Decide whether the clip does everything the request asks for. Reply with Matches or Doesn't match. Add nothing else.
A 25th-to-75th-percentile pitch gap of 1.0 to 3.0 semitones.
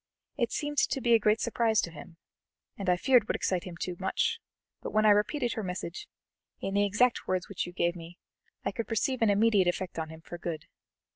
Doesn't match